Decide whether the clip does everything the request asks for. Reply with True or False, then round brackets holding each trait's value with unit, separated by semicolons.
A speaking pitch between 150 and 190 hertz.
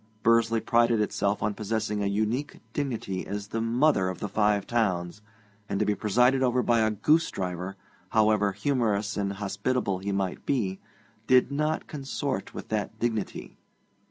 False (110 Hz)